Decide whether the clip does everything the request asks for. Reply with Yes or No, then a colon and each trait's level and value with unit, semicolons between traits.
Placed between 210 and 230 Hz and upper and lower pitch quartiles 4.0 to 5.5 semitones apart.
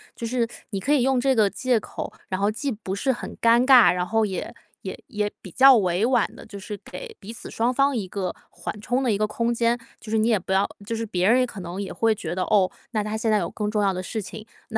No: high, 220 Hz; average, 3.4 semitones